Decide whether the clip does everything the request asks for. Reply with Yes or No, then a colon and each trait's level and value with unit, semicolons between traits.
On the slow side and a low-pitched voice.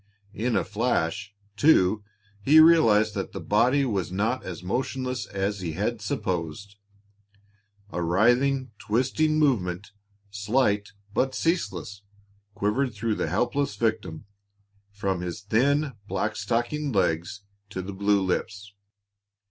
Yes: slow, 120 wpm; low, 105 Hz